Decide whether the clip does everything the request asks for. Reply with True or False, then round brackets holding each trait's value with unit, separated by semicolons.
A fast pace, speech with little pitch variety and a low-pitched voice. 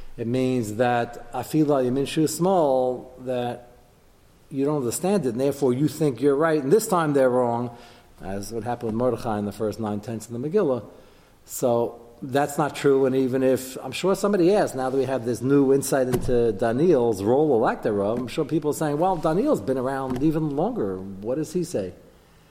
False (210 wpm; 3.6 semitones; 130 Hz)